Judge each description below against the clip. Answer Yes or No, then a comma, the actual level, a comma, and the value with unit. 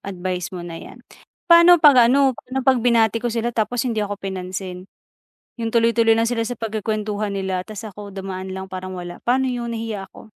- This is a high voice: Yes, high, 220 Hz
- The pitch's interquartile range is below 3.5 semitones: No, average, 3.8 semitones